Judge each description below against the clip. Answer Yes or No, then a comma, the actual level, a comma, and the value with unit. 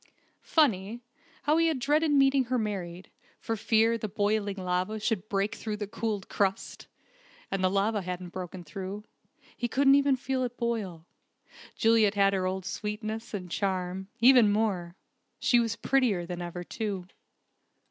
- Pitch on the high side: Yes, high, 210 Hz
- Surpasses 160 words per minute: No, average, 155 wpm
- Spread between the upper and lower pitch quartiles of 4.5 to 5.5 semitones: No, average, 3.8 semitones